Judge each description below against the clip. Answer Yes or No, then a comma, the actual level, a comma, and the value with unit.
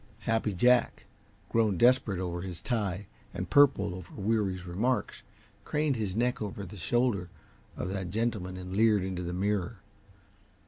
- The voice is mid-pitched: No, low, 100 Hz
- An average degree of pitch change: Yes, average, 3.8 semitones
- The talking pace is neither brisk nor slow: Yes, average, 145 wpm